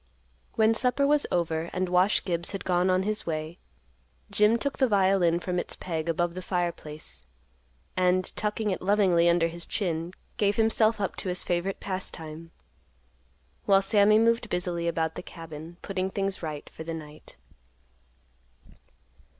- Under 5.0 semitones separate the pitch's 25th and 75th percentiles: Yes, average, 3.3 semitones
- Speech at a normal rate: Yes, average, 150 wpm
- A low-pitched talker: No, medium, 180 Hz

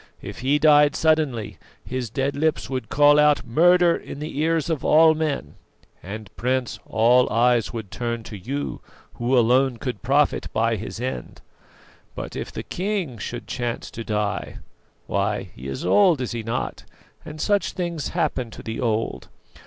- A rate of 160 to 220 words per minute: Yes, average, 165 wpm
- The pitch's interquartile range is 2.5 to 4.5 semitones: No, average, 5.0 semitones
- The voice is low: Yes, low, 130 Hz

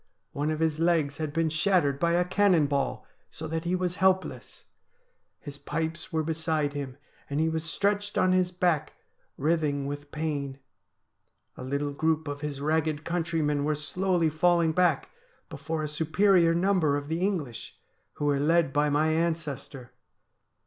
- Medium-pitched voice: Yes, medium, 160 Hz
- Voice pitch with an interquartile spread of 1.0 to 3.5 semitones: Yes, average, 2.8 semitones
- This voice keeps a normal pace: Yes, average, 165 wpm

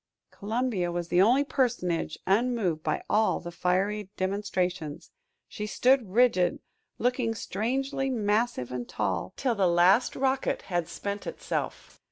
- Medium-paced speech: No, slow, 130 wpm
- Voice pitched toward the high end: Yes, high, 205 Hz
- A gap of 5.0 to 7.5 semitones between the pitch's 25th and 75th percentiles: Yes, wide, 5.4 semitones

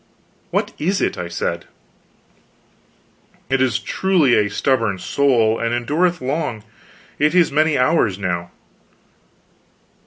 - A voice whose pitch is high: No, low, 130 Hz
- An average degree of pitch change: No, wide, 6.3 semitones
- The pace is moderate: No, slow, 115 wpm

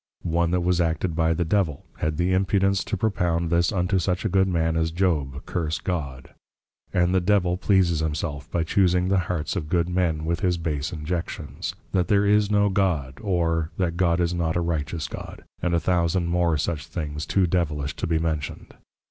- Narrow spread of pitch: Yes, narrow, 2.3 semitones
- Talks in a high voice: No, very low, 85 Hz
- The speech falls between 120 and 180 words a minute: No, average, 195 wpm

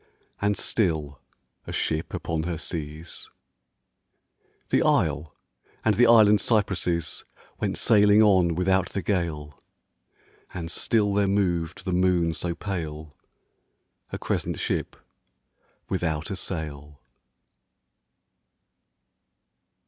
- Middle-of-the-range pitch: No, very low, 90 Hz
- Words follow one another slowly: Yes, slow, 100 wpm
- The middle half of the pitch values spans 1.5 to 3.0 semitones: No, average, 4.0 semitones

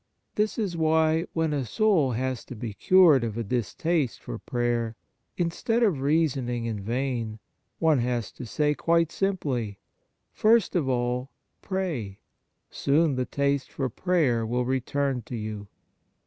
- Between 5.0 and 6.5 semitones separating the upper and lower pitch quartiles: Yes, wide, 5.4 semitones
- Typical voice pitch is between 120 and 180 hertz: Yes, low, 135 Hz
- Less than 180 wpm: Yes, average, 150 wpm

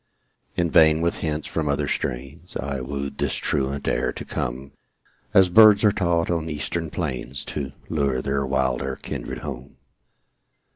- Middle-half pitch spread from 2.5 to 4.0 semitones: Yes, average, 3.7 semitones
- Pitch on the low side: Yes, very low, 70 Hz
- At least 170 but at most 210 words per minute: No, average, 150 wpm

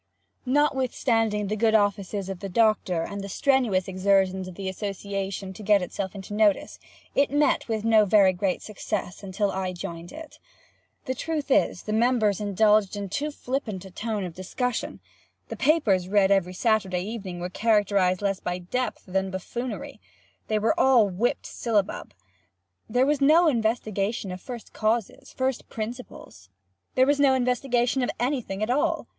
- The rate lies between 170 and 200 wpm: No, average, 160 wpm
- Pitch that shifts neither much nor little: Yes, average, 4.3 semitones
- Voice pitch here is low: No, high, 210 Hz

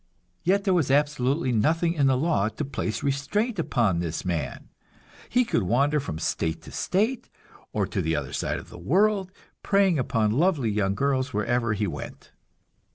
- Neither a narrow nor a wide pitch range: No, wide, 8.2 semitones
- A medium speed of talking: Yes, average, 170 wpm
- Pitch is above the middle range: No, low, 135 Hz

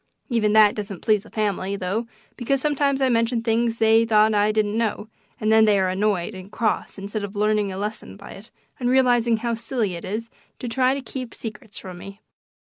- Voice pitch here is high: Yes, high, 220 Hz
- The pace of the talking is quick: Yes, fast, 210 wpm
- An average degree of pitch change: No, narrow, 2.3 semitones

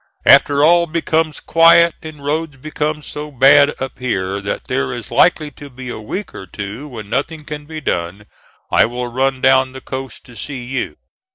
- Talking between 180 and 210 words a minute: Yes, average, 185 wpm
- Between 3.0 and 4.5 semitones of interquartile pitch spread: Yes, average, 3.8 semitones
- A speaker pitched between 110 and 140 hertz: Yes, low, 135 Hz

